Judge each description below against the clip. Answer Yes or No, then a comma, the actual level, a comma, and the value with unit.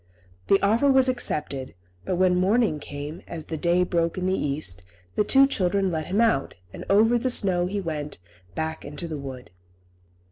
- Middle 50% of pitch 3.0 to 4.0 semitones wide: No, average, 5.1 semitones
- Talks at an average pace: Yes, average, 180 wpm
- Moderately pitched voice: Yes, medium, 180 Hz